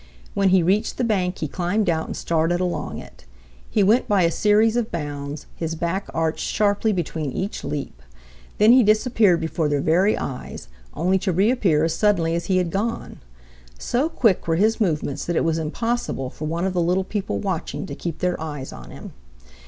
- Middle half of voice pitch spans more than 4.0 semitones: Yes, average, 4.5 semitones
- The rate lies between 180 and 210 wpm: Yes, average, 195 wpm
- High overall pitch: No, medium, 180 Hz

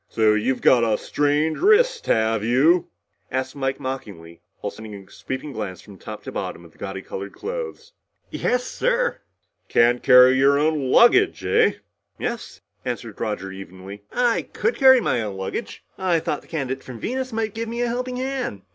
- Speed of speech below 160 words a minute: No, average, 175 wpm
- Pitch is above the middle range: No, low, 130 Hz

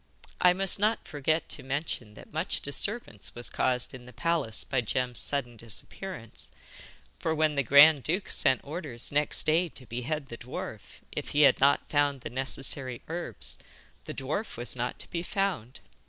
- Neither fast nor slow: Yes, average, 170 wpm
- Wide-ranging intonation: No, average, 4.5 semitones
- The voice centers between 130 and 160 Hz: Yes, medium, 140 Hz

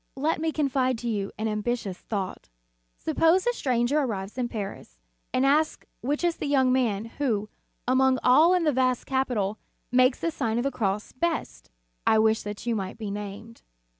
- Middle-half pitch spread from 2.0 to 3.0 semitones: No, average, 4.6 semitones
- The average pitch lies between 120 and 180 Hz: No, high, 245 Hz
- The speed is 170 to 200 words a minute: Yes, average, 180 wpm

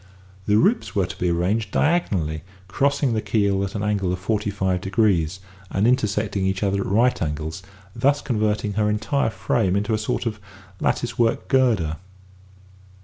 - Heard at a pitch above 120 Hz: No, low, 105 Hz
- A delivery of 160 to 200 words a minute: Yes, average, 165 wpm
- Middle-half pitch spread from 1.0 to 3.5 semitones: Yes, average, 3.2 semitones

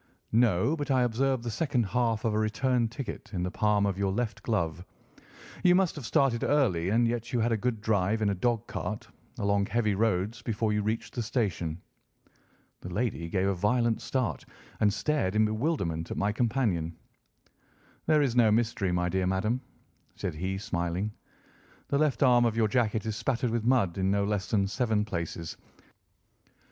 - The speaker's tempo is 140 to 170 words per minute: No, average, 180 wpm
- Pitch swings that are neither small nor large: Yes, average, 3.8 semitones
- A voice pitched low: Yes, low, 110 Hz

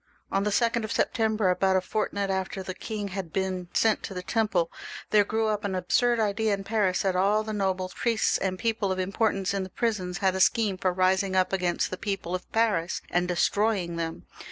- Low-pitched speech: No, high, 195 Hz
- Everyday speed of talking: No, fast, 215 wpm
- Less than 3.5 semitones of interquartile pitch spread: Yes, narrow, 2.6 semitones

